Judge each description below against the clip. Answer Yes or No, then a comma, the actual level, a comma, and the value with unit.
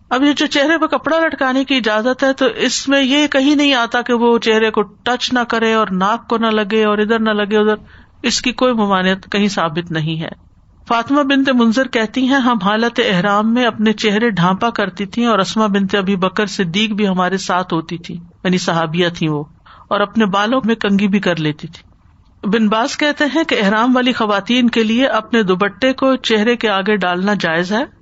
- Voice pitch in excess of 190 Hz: Yes, high, 220 Hz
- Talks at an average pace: No, fast, 210 wpm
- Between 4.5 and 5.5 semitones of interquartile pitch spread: No, average, 4.0 semitones